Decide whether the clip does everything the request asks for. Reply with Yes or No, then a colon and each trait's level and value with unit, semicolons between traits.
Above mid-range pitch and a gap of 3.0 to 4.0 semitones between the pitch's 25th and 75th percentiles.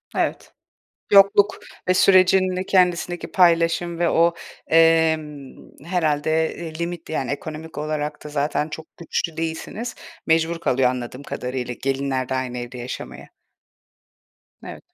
No: medium, 160 Hz; average, 3.4 semitones